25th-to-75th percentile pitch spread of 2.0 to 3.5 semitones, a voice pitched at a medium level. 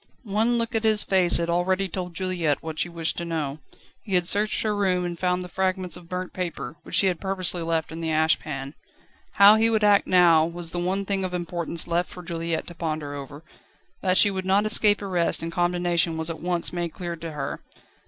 Yes: narrow, 2.4 semitones; medium, 175 Hz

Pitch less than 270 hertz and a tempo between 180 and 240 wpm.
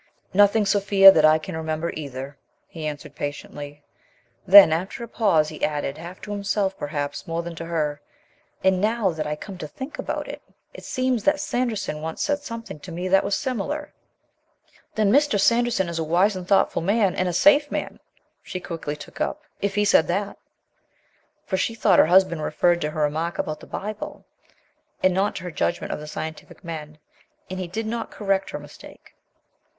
Yes: medium, 185 Hz; average, 190 wpm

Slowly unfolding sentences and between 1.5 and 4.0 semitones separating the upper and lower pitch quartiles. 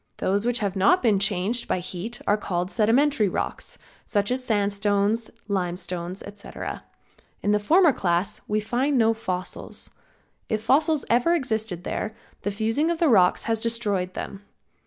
No: average, 155 wpm; average, 3.5 semitones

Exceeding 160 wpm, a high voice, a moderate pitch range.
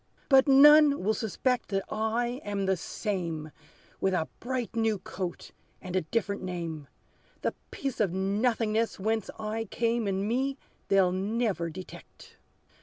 No: average, 140 wpm; high, 215 Hz; average, 3.9 semitones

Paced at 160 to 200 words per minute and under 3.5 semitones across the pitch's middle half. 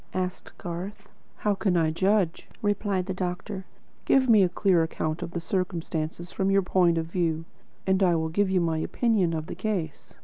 Yes: average, 190 wpm; average, 2.9 semitones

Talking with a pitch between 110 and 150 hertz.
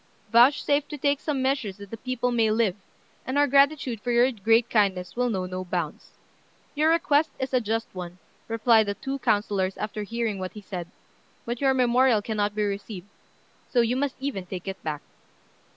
No: high, 225 Hz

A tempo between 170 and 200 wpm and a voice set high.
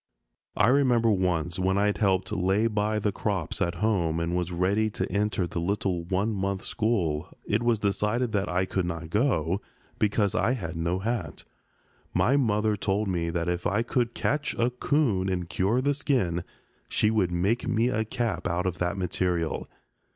No: average, 180 wpm; low, 100 Hz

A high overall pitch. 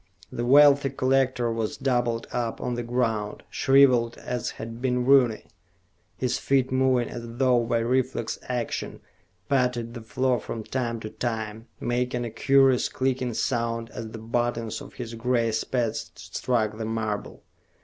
No: low, 120 Hz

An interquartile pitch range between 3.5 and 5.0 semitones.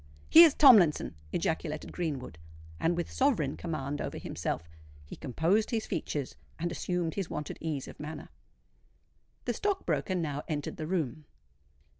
Yes: average, 4.0 semitones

